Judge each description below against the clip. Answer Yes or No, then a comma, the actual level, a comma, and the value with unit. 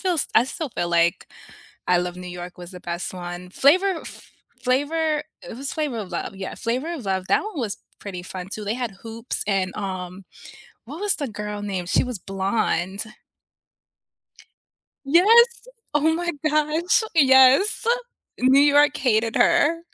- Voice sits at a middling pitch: No, high, 230 Hz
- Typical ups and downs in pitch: No, wide, 8.1 semitones